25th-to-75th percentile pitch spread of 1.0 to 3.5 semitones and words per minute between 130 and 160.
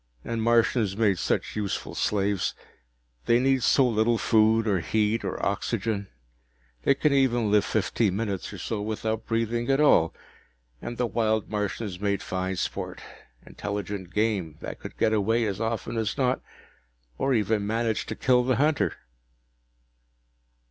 Yes: narrow, 2.4 semitones; average, 150 wpm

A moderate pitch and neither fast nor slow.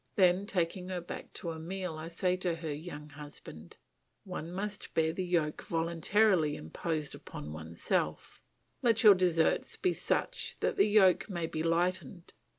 Yes: medium, 170 Hz; average, 155 wpm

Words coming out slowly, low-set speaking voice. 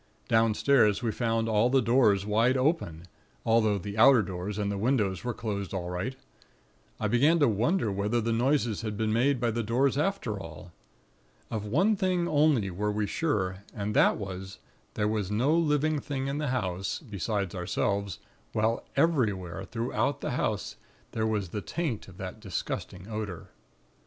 No: average, 165 wpm; low, 110 Hz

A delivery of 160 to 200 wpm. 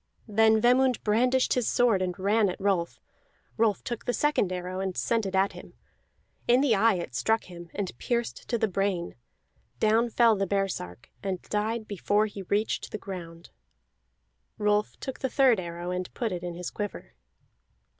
Yes: average, 175 wpm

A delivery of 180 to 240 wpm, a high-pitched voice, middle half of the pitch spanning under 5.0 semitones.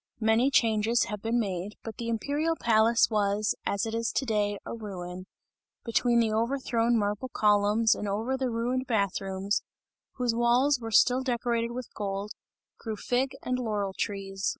No: average, 165 wpm; high, 225 Hz; average, 2.7 semitones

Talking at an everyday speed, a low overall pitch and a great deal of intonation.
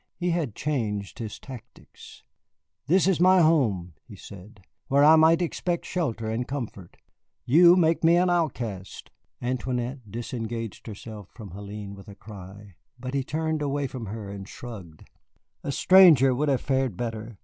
Yes: average, 155 wpm; low, 125 Hz; wide, 6.9 semitones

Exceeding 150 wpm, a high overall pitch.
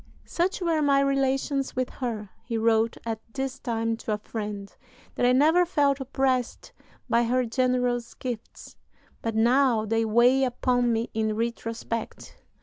No: average, 145 wpm; high, 245 Hz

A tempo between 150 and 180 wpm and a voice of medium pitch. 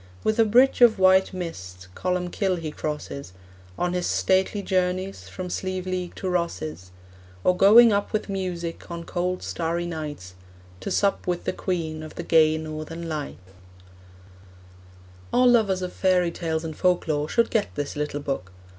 Yes: average, 155 wpm; medium, 175 Hz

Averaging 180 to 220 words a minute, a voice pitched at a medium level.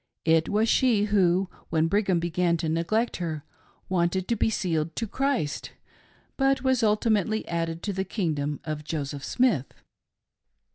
No: average, 145 wpm; medium, 180 Hz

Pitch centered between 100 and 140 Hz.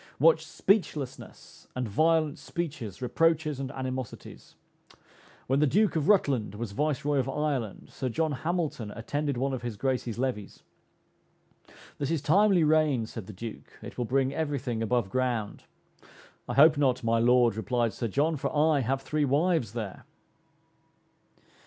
Yes: low, 135 Hz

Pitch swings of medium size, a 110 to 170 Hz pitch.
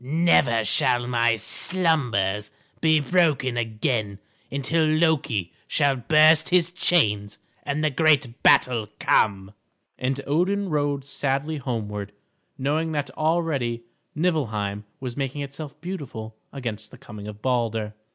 No: wide, 5.8 semitones; low, 135 Hz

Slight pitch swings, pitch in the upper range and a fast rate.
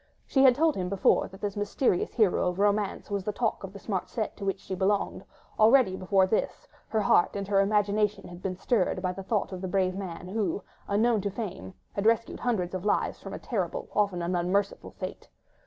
Yes: narrow, 2.3 semitones; high, 200 Hz; fast, 215 wpm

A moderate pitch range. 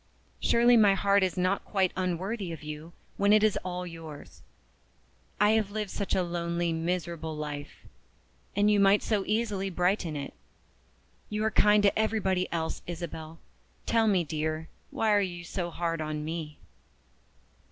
Yes: average, 3.9 semitones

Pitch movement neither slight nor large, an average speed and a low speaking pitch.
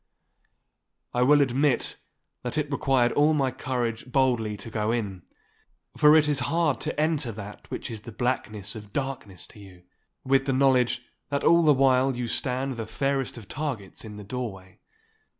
Yes: average, 3.8 semitones; average, 170 wpm; low, 125 Hz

